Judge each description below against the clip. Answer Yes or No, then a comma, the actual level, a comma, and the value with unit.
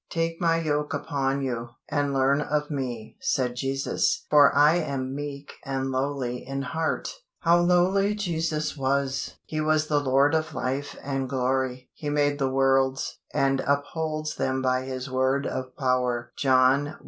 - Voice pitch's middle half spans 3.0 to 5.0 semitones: No, narrow, 2.5 semitones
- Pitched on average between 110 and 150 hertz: Yes, medium, 140 Hz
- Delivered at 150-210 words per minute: Yes, average, 160 wpm